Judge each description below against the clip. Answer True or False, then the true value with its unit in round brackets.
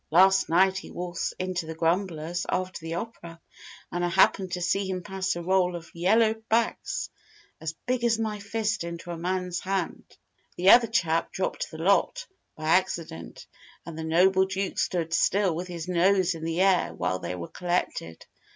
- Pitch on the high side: False (180 Hz)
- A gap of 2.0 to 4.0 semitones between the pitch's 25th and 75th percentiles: True (2.5 semitones)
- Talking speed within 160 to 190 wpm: True (180 wpm)